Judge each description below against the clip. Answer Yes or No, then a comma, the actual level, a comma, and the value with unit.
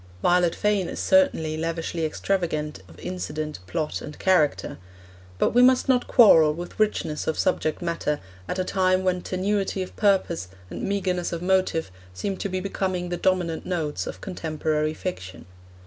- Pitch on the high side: No, medium, 180 Hz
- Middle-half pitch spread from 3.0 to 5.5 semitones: Yes, average, 3.3 semitones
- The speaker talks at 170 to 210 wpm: No, average, 160 wpm